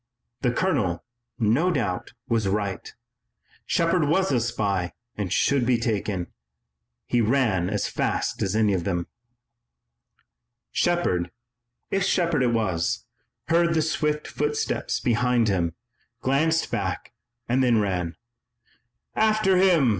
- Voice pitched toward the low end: Yes, low, 120 Hz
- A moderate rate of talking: No, slow, 120 wpm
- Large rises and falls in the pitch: Yes, wide, 8.3 semitones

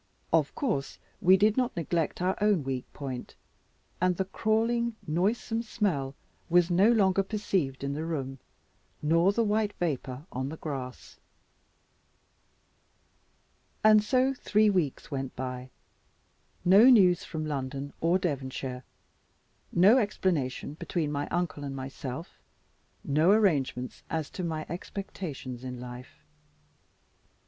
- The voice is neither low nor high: Yes, medium, 165 Hz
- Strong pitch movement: Yes, wide, 6.8 semitones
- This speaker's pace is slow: Yes, slow, 120 wpm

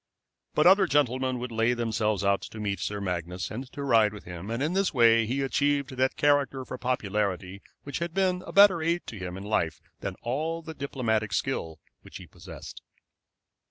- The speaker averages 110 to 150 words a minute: No, average, 195 wpm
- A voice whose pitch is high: No, low, 125 Hz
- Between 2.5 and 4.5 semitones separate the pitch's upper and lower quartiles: No, wide, 5.6 semitones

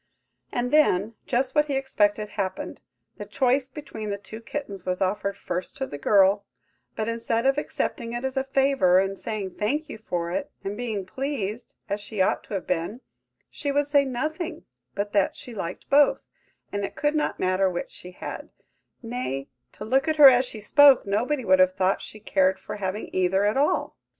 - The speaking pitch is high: Yes, high, 215 Hz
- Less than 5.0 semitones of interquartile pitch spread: No, wide, 5.6 semitones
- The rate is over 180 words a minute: Yes, average, 190 wpm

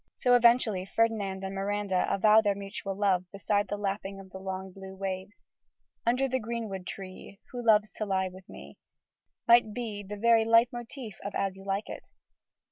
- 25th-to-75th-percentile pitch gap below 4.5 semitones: Yes, average, 2.8 semitones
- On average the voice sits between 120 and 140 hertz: No, high, 205 Hz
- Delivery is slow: No, average, 180 wpm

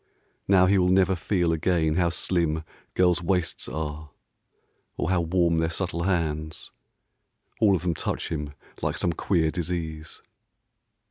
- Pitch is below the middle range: Yes, very low, 85 Hz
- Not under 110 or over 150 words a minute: Yes, average, 140 wpm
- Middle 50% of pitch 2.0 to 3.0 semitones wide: Yes, narrow, 2.4 semitones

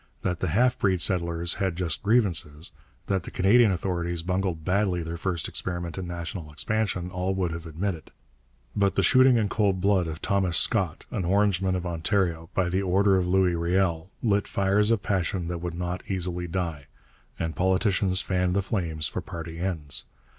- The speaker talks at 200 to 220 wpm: No, average, 175 wpm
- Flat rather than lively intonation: Yes, narrow, 2.3 semitones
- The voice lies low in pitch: Yes, very low, 90 Hz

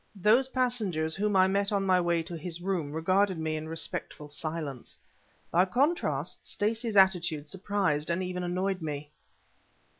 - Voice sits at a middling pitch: Yes, medium, 180 Hz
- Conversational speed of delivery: Yes, average, 150 wpm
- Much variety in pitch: No, average, 3.8 semitones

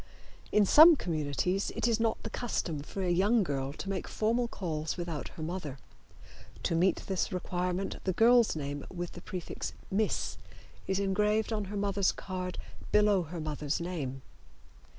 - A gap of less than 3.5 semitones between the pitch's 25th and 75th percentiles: No, average, 4.3 semitones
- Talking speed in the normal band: Yes, average, 160 wpm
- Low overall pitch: No, medium, 185 Hz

